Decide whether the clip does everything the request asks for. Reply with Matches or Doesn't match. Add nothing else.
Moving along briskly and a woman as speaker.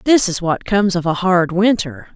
Matches